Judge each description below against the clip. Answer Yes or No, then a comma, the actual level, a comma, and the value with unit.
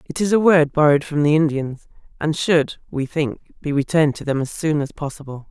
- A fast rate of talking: Yes, fast, 220 wpm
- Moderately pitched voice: Yes, medium, 150 Hz